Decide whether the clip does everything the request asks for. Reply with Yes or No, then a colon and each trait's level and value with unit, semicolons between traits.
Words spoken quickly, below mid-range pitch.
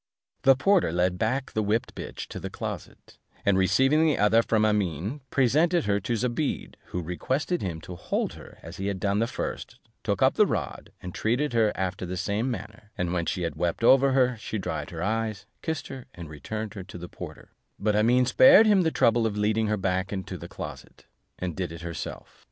Yes: fast, 210 wpm; low, 105 Hz